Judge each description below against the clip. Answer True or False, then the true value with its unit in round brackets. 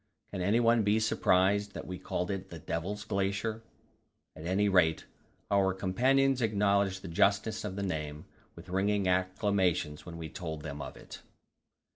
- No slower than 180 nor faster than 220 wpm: False (155 wpm)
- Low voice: True (95 Hz)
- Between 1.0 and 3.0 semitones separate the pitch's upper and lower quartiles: True (2.6 semitones)